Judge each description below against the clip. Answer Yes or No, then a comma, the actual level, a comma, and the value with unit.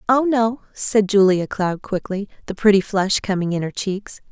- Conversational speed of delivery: Yes, average, 180 wpm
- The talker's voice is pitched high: Yes, high, 200 Hz